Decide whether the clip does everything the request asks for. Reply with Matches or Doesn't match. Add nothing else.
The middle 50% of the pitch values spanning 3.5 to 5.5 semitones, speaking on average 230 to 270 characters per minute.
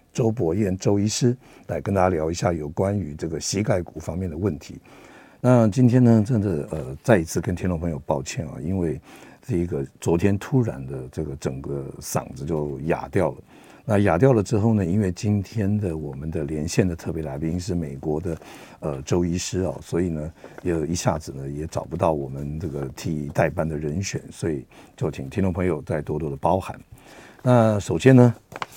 Doesn't match